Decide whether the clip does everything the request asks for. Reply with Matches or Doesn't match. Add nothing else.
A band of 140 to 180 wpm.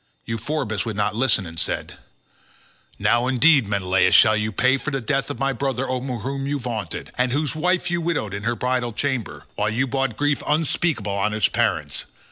Doesn't match